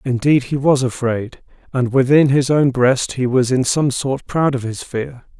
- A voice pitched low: Yes, low, 130 Hz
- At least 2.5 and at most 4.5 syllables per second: Yes, 4.3 syllables/s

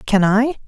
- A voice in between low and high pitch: No, high, 225 Hz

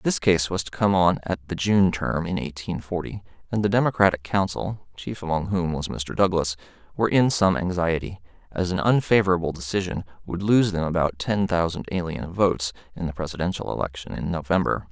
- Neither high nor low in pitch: No, very low, 90 Hz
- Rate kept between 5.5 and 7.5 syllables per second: Yes, 5.6 syllables/s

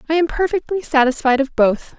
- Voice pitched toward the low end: No, very high, 295 Hz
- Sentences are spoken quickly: No, average, 180 wpm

